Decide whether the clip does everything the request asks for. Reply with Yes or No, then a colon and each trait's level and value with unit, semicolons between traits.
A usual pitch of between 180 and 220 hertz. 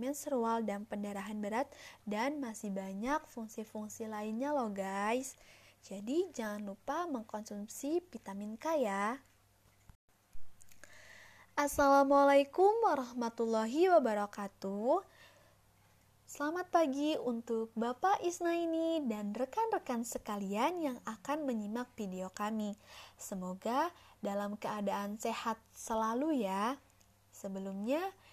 No: high, 230 Hz